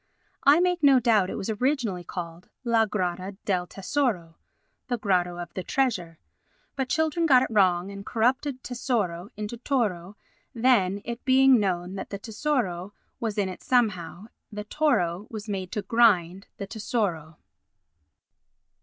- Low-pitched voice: No, high, 210 Hz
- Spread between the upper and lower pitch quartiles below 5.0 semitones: No, average, 5.3 semitones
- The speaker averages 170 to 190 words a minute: No, average, 145 wpm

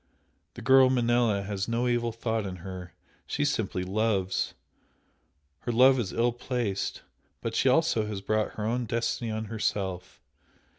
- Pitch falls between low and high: No, low, 110 Hz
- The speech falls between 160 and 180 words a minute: No, average, 150 wpm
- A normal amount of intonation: Yes, average, 3.3 semitones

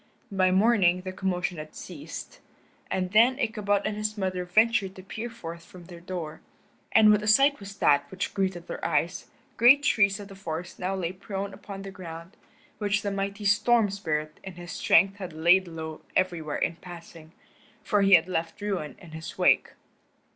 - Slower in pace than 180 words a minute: No, average, 185 wpm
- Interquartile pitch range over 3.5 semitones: No, average, 3.0 semitones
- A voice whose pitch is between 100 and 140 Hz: No, high, 190 Hz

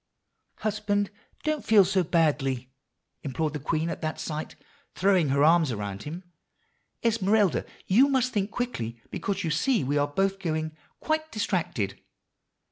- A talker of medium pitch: Yes, medium, 170 Hz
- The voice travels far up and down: Yes, wide, 5.9 semitones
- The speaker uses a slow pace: No, average, 145 wpm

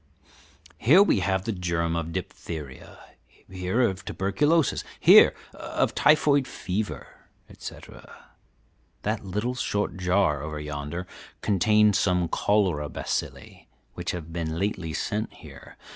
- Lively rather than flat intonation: No, average, 4.2 semitones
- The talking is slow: Yes, slow, 115 wpm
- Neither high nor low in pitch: No, very low, 95 Hz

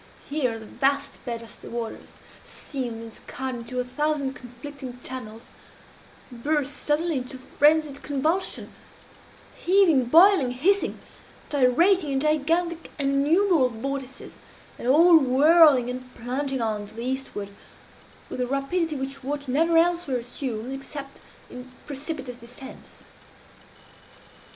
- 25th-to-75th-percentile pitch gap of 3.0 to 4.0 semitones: Yes, average, 3.5 semitones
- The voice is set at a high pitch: Yes, very high, 270 Hz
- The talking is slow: Yes, slow, 120 wpm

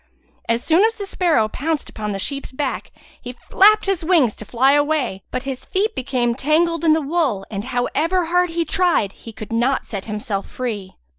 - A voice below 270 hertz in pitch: No, very high, 275 Hz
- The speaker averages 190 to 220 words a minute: Yes, average, 195 wpm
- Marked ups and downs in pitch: Yes, wide, 6.5 semitones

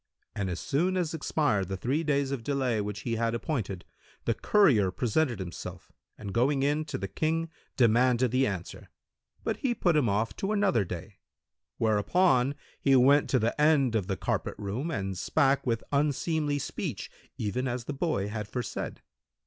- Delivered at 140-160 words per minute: No, average, 175 wpm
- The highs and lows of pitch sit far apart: Yes, wide, 5.9 semitones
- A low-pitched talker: Yes, low, 125 Hz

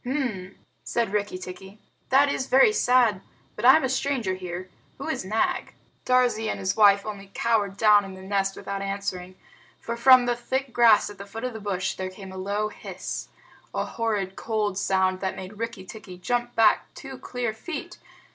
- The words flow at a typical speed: Yes, average, 190 wpm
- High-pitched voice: Yes, high, 210 Hz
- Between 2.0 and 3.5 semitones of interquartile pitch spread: No, average, 3.9 semitones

